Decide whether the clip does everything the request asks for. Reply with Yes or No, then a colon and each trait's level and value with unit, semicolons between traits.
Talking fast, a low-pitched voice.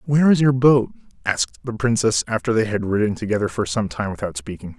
Yes: fast, 215 wpm; low, 110 Hz